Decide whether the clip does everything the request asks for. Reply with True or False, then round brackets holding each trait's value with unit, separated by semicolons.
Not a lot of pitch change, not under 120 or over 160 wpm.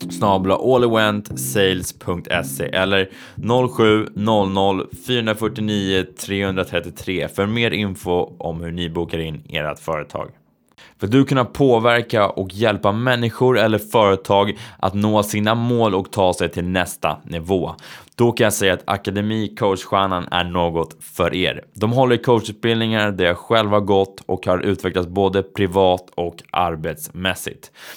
False (3.4 semitones; 130 wpm)